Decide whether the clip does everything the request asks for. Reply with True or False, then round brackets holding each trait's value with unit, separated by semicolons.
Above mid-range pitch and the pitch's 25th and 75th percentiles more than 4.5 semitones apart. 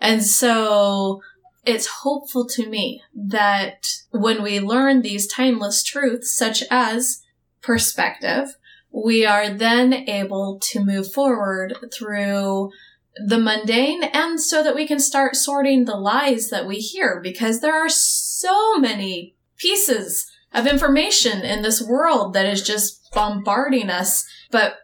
True (230 Hz; 5.0 semitones)